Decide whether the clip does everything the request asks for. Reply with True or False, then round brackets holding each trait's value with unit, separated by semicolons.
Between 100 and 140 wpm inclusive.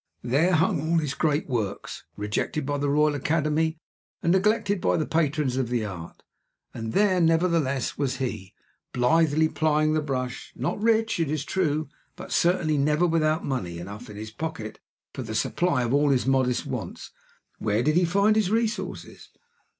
False (165 wpm)